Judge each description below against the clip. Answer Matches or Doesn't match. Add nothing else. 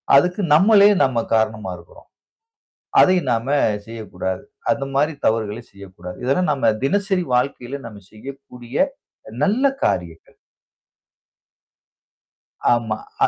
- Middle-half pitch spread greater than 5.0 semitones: Matches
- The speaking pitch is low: Matches